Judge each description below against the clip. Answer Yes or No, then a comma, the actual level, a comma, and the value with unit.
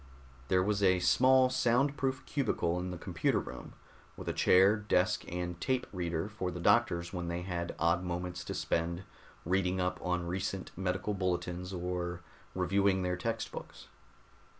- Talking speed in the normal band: Yes, average, 160 wpm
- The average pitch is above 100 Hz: No, very low, 90 Hz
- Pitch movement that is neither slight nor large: No, narrow, 2.2 semitones